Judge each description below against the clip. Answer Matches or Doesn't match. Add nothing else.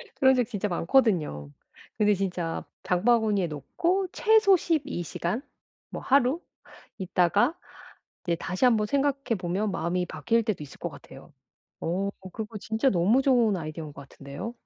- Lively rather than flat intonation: Matches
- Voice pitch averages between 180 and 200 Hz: Doesn't match